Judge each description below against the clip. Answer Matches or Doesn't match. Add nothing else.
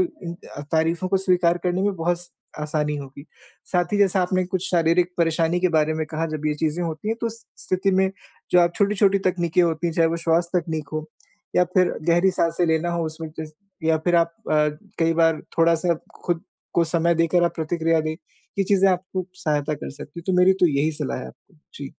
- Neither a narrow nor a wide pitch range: Doesn't match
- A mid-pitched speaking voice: Matches